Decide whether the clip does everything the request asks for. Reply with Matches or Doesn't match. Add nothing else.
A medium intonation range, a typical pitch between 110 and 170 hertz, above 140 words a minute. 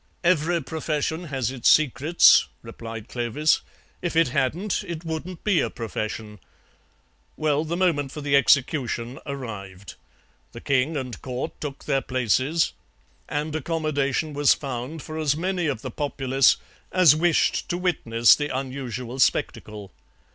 Doesn't match